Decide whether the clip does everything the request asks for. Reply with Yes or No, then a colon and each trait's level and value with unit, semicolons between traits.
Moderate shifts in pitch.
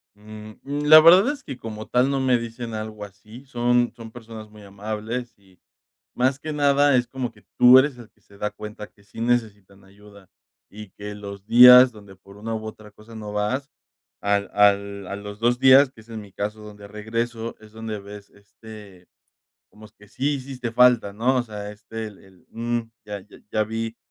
Yes: average, 3.0 semitones